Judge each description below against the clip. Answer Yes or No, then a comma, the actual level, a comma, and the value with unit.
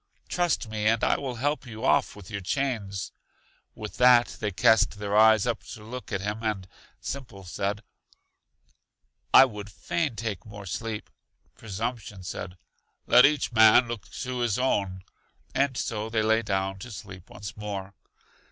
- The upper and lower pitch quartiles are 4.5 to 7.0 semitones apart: No, average, 3.2 semitones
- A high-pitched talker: No, low, 110 Hz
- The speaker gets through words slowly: No, average, 160 wpm